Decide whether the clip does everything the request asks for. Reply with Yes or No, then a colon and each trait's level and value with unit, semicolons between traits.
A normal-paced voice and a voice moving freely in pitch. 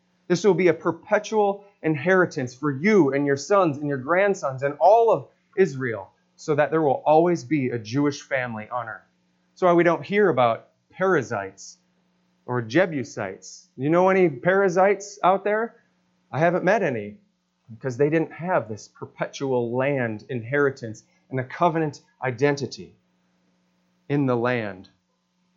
Yes: average, 150 wpm; wide, 6.9 semitones